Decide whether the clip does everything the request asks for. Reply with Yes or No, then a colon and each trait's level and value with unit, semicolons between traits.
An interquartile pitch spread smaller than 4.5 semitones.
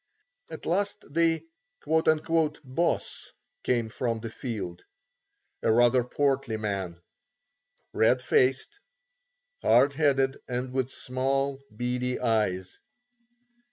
Yes: average, 3.6 semitones